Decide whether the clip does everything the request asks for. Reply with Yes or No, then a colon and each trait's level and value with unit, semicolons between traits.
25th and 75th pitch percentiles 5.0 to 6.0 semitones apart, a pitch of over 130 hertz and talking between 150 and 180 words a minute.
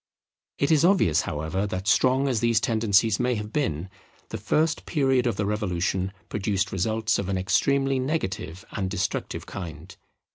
No: wide, 5.5 semitones; low, 105 Hz; average, 155 wpm